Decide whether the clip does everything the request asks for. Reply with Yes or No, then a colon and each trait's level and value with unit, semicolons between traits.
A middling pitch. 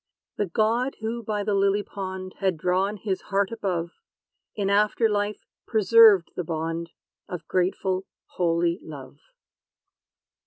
No: high, 195 Hz